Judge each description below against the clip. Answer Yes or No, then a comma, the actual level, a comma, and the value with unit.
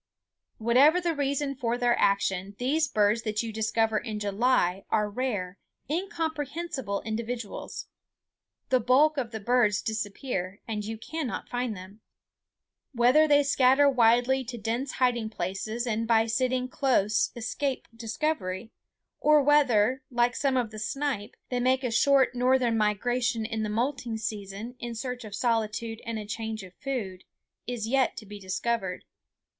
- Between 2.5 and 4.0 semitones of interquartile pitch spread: Yes, average, 3.4 semitones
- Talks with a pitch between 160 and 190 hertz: No, high, 235 Hz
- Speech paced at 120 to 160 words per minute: Yes, average, 150 wpm